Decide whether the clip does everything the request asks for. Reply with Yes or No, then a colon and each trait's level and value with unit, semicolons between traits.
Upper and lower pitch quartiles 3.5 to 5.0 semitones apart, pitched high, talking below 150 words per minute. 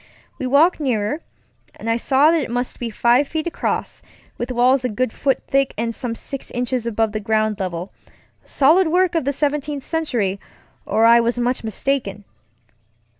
No: average, 3.9 semitones; very high, 250 Hz; average, 170 wpm